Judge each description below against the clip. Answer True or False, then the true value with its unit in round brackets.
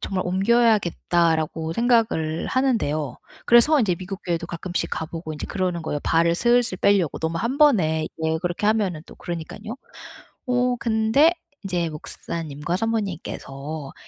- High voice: False (180 Hz)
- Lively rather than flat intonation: True (5.8 semitones)